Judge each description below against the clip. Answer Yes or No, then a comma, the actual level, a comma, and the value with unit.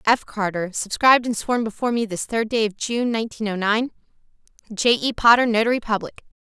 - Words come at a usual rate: Yes, average, 185 wpm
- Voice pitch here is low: No, high, 220 Hz